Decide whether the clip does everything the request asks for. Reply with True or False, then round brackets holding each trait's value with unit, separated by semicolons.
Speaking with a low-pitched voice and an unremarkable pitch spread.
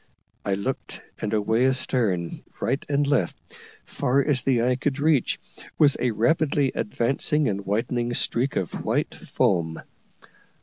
True (125 Hz; 4.9 semitones)